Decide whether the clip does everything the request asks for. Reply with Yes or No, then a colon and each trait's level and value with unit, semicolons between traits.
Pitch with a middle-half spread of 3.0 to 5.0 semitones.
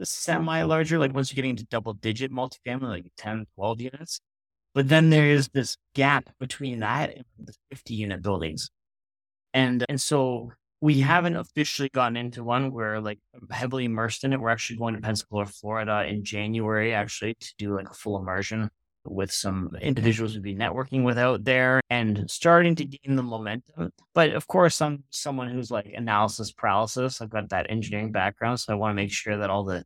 Yes: average, 4.1 semitones